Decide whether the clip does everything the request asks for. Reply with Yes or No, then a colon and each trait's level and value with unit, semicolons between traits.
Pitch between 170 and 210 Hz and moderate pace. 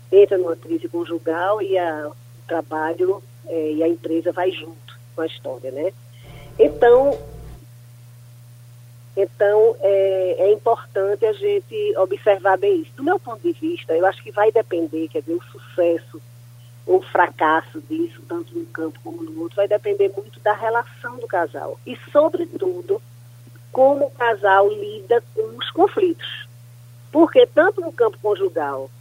Yes: medium, 185 Hz; average, 150 wpm